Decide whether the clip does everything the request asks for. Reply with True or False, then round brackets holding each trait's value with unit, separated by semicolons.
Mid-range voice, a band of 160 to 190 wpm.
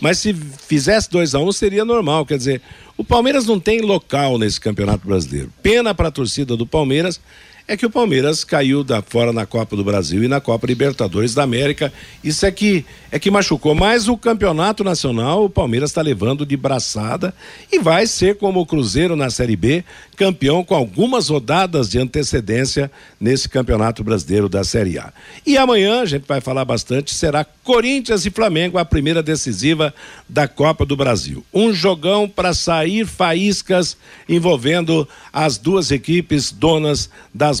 True (150 Hz; 170 wpm)